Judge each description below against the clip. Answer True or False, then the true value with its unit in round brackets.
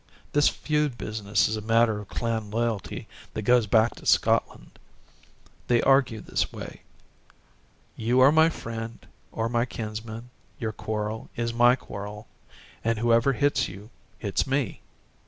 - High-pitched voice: False (115 Hz)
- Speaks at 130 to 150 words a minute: True (140 wpm)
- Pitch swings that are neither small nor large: False (2.2 semitones)